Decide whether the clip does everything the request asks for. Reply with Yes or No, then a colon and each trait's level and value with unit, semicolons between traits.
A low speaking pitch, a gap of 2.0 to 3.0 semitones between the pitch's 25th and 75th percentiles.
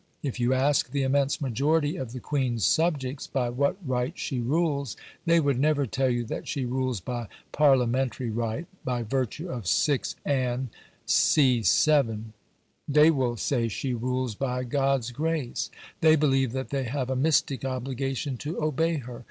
Yes: low, 130 Hz; average, 2.7 semitones